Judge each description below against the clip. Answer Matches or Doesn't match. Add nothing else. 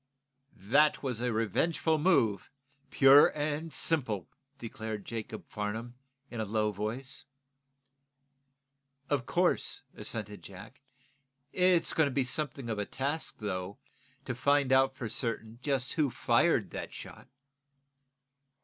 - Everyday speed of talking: Doesn't match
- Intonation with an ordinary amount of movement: Matches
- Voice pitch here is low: Matches